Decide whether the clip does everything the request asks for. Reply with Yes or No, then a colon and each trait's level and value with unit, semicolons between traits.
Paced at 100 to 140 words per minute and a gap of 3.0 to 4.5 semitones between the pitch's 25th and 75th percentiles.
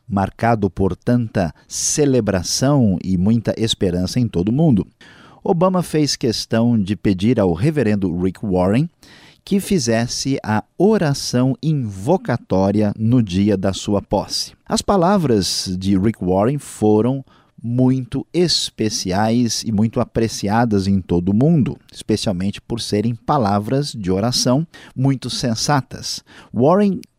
No: slow, 120 wpm; average, 5.1 semitones